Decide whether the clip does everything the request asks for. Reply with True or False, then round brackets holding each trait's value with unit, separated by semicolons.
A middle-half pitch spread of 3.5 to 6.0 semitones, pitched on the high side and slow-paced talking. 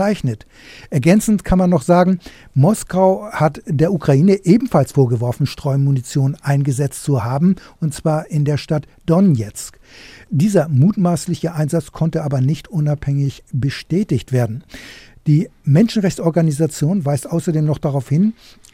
False (4.2 semitones; 155 Hz; 120 wpm)